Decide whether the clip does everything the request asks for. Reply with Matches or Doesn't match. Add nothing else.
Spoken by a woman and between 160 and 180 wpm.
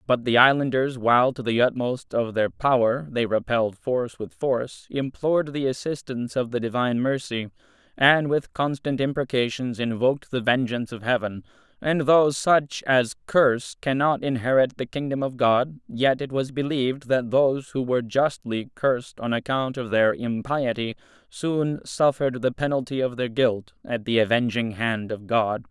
Doesn't match